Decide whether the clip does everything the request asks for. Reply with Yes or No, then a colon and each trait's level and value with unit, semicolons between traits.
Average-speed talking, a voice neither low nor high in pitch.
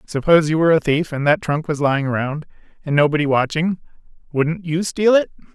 Yes: average, 185 wpm; medium, 155 Hz